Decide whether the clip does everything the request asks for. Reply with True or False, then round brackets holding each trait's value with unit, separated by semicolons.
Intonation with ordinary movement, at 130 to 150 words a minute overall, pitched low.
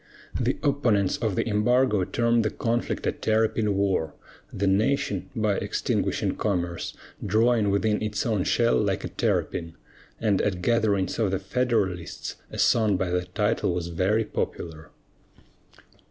True (3.2 semitones; 140 wpm; 105 Hz)